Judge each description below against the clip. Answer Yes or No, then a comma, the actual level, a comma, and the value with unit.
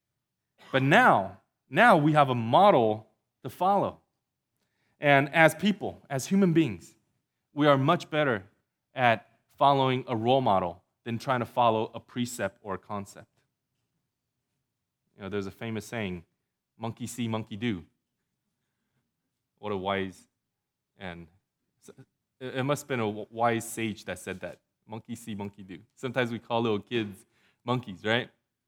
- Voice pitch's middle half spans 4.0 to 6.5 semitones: Yes, average, 4.3 semitones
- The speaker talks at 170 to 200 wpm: No, average, 140 wpm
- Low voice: Yes, low, 115 Hz